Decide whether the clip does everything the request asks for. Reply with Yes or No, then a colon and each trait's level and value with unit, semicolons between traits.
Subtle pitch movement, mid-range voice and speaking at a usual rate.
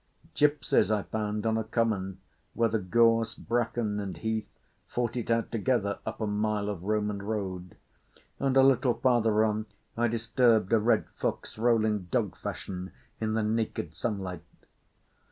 No: narrow, 2.0 semitones; low, 110 Hz; average, 155 wpm